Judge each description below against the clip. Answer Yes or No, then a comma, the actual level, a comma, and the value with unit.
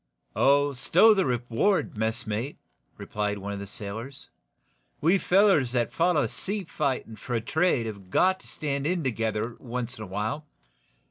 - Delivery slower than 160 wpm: Yes, average, 150 wpm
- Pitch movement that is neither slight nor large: No, wide, 6.0 semitones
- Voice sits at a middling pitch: No, low, 125 Hz